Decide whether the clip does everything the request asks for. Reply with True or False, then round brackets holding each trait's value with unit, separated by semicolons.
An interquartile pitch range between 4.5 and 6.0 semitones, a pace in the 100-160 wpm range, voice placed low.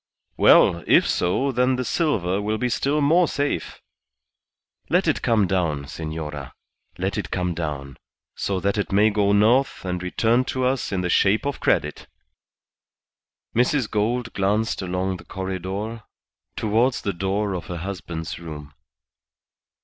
True (4.9 semitones; 145 wpm; 100 Hz)